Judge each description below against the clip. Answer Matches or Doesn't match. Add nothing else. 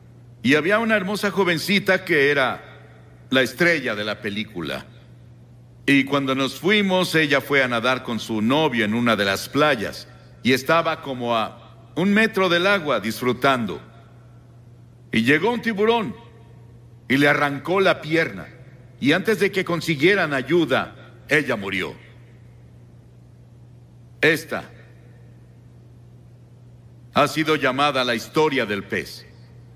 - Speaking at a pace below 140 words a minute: Matches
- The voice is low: Matches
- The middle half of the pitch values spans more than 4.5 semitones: Matches